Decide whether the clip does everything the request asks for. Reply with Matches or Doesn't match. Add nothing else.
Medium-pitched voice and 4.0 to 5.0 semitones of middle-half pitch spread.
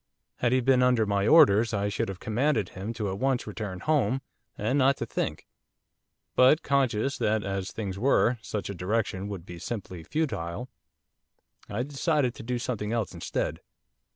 Doesn't match